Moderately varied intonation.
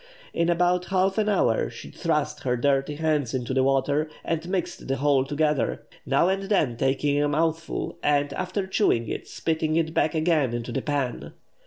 Yes: average, 3.7 semitones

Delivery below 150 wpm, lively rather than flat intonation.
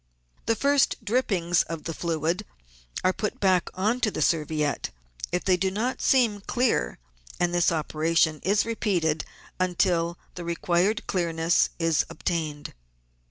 No: slow, 135 wpm; average, 3.8 semitones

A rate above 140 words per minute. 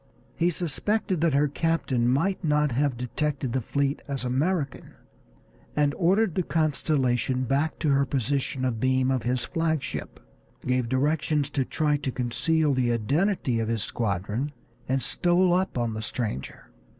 Yes: average, 150 wpm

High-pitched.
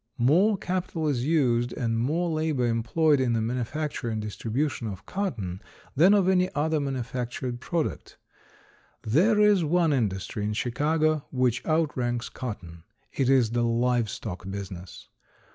No: low, 125 Hz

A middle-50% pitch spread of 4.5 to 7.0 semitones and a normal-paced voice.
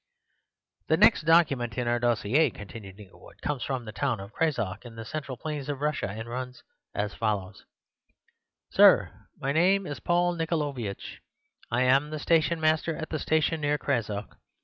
Yes: wide, 5.6 semitones; average, 155 wpm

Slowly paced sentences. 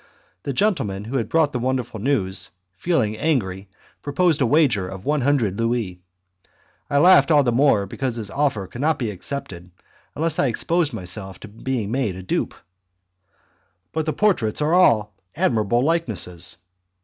No: average, 160 wpm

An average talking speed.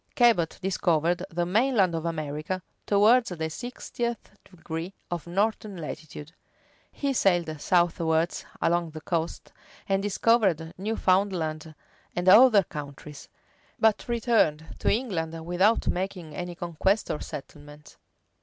No: slow, 115 wpm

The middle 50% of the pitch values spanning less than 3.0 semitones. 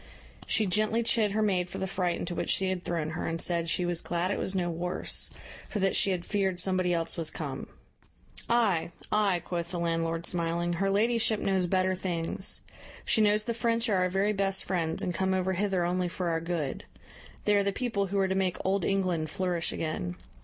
Yes: narrow, 2.6 semitones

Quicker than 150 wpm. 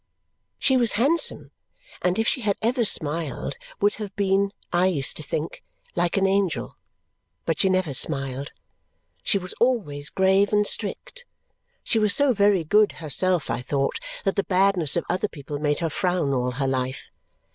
Yes: average, 170 wpm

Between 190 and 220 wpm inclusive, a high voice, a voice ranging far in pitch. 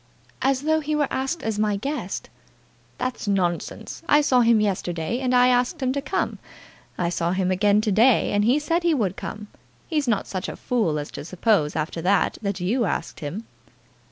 Yes: average, 195 wpm; high, 220 Hz; wide, 5.9 semitones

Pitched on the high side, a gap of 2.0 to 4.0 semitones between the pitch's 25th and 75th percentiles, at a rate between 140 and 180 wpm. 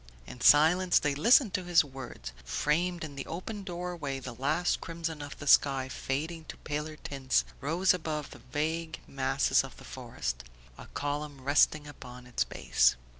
No: medium, 150 Hz; average, 3.6 semitones; average, 170 wpm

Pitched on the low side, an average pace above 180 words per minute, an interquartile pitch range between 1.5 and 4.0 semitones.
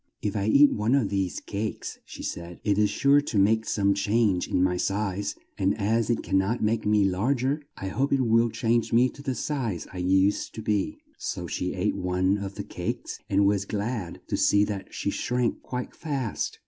Yes: low, 105 Hz; fast, 205 wpm; average, 3.3 semitones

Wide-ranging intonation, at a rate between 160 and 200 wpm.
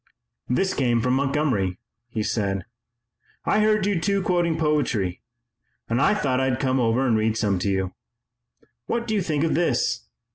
Yes: wide, 7.5 semitones; average, 170 wpm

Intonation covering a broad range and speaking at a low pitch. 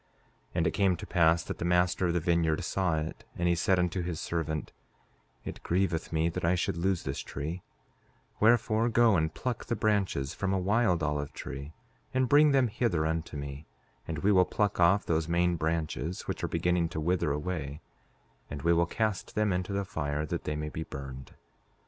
No: average, 3.4 semitones; very low, 85 Hz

